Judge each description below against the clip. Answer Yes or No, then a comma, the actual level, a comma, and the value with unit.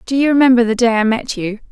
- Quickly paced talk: Yes, fast, 280 wpm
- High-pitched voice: Yes, high, 240 Hz